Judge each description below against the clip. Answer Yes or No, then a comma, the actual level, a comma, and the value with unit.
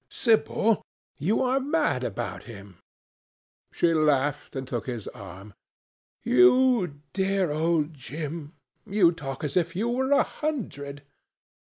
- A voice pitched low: No, medium, 155 Hz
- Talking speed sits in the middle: No, slow, 125 wpm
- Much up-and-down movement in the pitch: Yes, wide, 7.8 semitones